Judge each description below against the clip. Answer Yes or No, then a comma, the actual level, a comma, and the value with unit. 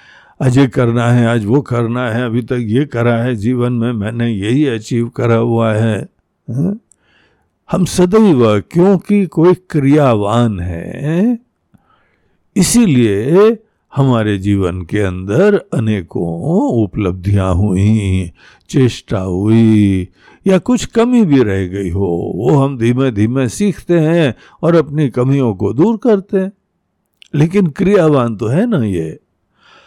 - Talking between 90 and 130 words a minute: Yes, average, 125 wpm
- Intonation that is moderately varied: No, wide, 8.0 semitones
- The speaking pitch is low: Yes, low, 125 Hz